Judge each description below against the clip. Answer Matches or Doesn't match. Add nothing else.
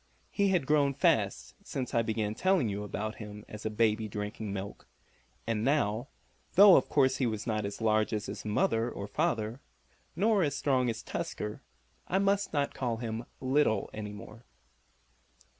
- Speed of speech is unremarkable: Matches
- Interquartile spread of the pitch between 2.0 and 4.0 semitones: Doesn't match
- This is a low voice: Matches